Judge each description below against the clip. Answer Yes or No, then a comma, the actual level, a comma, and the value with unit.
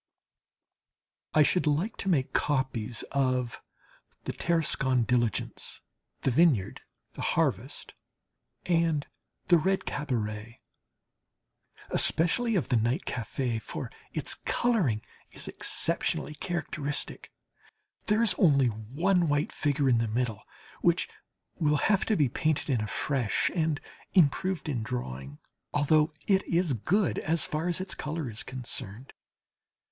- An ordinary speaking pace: No, slow, 120 wpm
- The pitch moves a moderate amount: No, wide, 5.8 semitones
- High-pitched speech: No, medium, 145 Hz